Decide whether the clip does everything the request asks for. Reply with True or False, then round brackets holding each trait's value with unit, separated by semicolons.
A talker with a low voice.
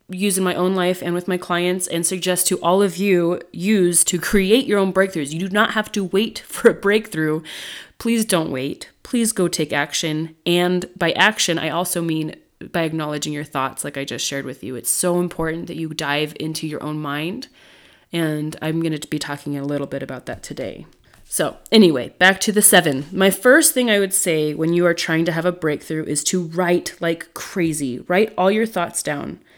False (175 Hz)